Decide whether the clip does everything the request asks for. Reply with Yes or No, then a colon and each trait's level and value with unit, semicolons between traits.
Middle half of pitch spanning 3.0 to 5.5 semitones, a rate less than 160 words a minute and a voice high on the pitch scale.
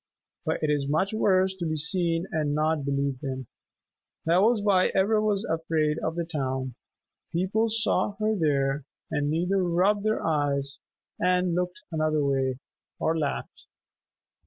No: average, 4.6 semitones; average, 150 wpm; medium, 165 Hz